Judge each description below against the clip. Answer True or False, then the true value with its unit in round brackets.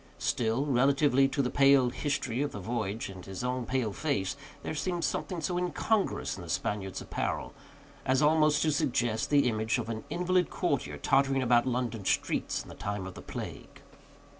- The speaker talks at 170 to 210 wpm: True (180 wpm)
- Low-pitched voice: True (130 Hz)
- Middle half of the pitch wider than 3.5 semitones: True (4.7 semitones)